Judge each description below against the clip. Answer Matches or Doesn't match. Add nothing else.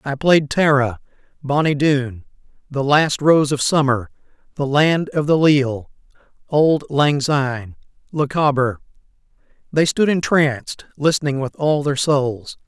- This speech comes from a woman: Doesn't match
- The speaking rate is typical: Doesn't match